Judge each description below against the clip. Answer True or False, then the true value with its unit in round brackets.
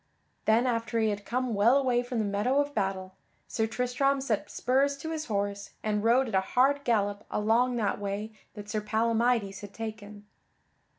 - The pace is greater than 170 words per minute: True (180 wpm)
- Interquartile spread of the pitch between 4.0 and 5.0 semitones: False (3.4 semitones)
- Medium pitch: False (225 Hz)